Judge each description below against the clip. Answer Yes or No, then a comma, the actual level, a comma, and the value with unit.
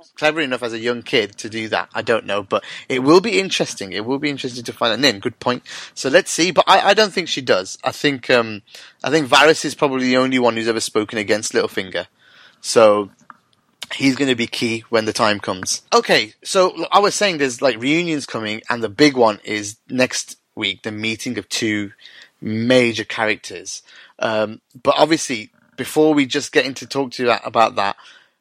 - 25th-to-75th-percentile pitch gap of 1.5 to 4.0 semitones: No, average, 5.1 semitones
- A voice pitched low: Yes, low, 130 Hz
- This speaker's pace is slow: No, fast, 205 wpm